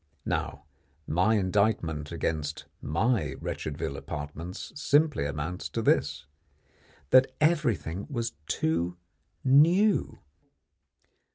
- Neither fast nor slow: No, slow, 85 wpm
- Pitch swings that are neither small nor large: No, wide, 8.7 semitones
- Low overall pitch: Yes, very low, 90 Hz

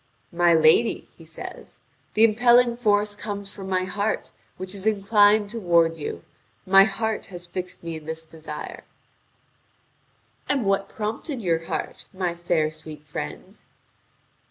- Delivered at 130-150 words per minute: Yes, slow, 135 wpm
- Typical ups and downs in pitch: Yes, average, 4.1 semitones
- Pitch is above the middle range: Yes, high, 195 Hz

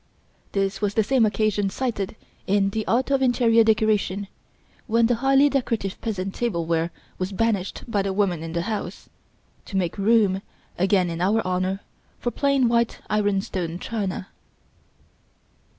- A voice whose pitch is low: No, high, 205 Hz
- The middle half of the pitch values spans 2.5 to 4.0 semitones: Yes, average, 3.3 semitones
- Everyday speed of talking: Yes, average, 145 wpm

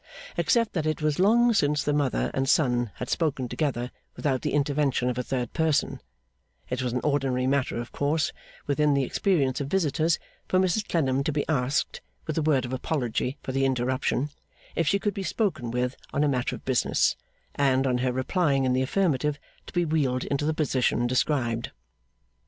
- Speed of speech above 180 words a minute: Yes, average, 190 wpm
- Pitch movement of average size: Yes, average, 3.4 semitones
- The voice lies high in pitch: No, medium, 140 Hz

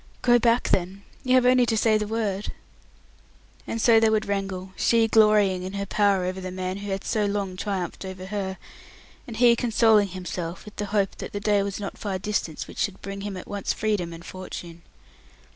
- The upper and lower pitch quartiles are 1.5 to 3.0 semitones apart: Yes, narrow, 2.5 semitones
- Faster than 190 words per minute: Yes, fast, 205 wpm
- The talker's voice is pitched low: No, high, 200 Hz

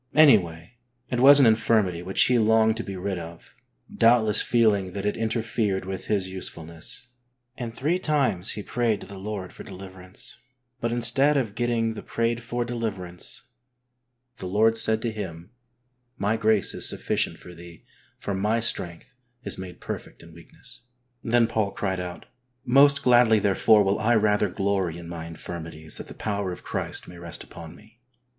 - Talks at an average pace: Yes, average, 170 wpm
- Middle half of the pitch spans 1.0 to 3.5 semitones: No, average, 4.1 semitones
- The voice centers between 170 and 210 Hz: No, low, 105 Hz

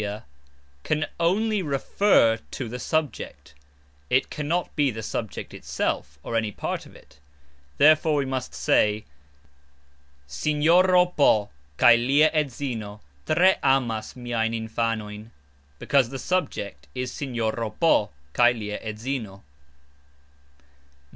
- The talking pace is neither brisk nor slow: No, slow, 115 wpm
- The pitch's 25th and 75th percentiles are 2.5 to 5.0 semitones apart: No, wide, 5.6 semitones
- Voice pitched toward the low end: Yes, low, 120 Hz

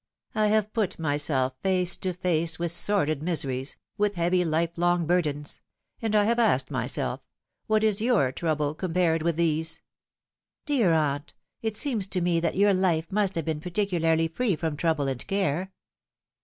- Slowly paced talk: No, average, 175 wpm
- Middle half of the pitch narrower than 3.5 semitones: No, average, 4.0 semitones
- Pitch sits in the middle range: Yes, medium, 170 Hz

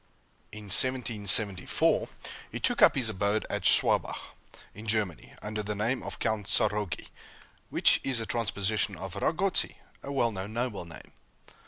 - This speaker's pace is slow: No, average, 145 wpm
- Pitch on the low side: Yes, low, 105 Hz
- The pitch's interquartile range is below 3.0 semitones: Yes, narrow, 2.5 semitones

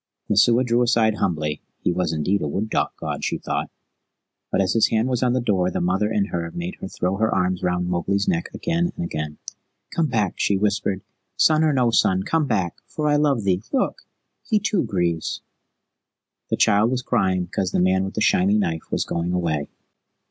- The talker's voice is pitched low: Yes, low, 100 Hz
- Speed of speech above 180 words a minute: Yes, average, 200 wpm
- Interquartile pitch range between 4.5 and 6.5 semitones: Yes, average, 5.1 semitones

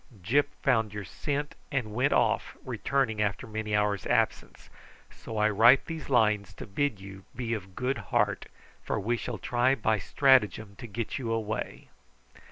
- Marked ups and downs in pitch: No, average, 3.7 semitones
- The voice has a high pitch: No, low, 110 Hz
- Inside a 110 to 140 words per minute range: No, average, 165 wpm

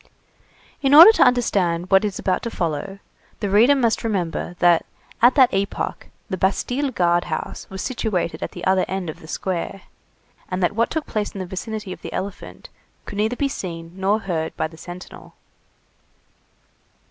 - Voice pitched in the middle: No, high, 195 Hz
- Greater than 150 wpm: Yes, average, 175 wpm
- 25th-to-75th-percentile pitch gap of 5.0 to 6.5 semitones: No, average, 4.2 semitones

